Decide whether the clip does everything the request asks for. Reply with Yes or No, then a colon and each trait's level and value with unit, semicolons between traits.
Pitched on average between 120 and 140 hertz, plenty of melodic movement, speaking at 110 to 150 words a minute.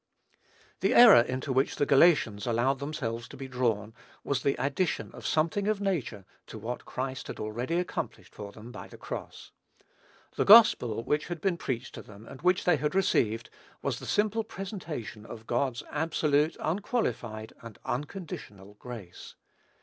No: low, 135 Hz; wide, 6.8 semitones; average, 160 wpm